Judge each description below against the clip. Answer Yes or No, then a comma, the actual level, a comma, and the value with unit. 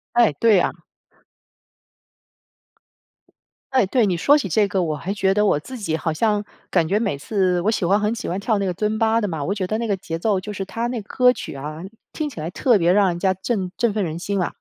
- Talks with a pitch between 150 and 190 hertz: No, high, 200 Hz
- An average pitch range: Yes, average, 3.8 semitones